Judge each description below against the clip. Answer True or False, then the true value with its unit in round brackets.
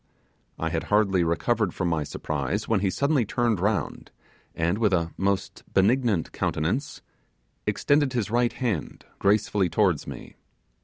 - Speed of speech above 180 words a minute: False (140 wpm)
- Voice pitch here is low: True (100 Hz)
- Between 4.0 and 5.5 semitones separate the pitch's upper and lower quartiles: True (5.1 semitones)